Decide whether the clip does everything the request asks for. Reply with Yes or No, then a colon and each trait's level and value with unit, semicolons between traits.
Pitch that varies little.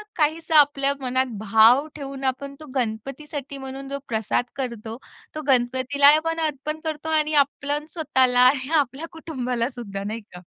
No: average, 3.2 semitones